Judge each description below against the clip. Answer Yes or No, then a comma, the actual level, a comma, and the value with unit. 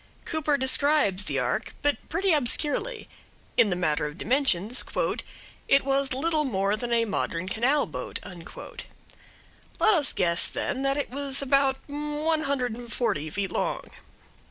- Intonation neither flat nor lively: No, wide, 6.4 semitones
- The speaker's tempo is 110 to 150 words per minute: Yes, average, 145 wpm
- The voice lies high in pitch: Yes, very high, 265 Hz